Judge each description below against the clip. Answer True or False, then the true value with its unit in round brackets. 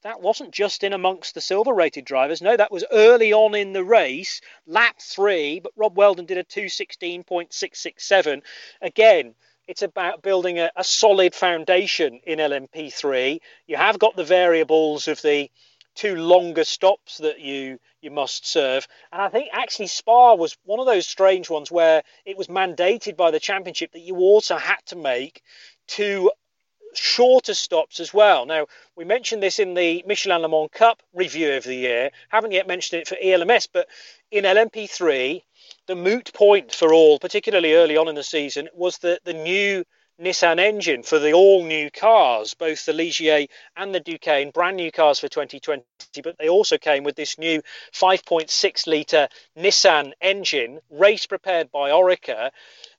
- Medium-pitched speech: True (180 Hz)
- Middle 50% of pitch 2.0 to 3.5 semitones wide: False (4.6 semitones)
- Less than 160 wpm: False (170 wpm)